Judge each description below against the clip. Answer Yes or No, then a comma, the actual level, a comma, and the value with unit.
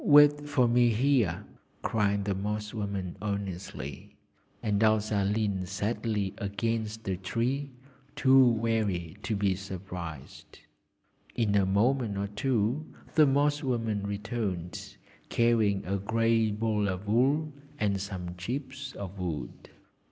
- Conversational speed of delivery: No, slow, 120 wpm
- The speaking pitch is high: No, low, 105 Hz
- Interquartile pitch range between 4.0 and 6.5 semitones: No, average, 3.1 semitones